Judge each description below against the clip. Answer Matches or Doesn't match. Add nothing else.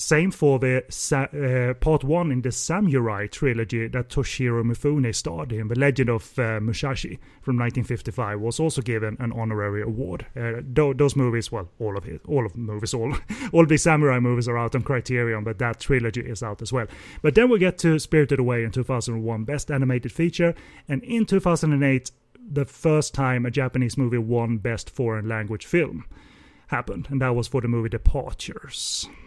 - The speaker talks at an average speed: Matches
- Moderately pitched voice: Doesn't match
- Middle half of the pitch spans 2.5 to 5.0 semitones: Matches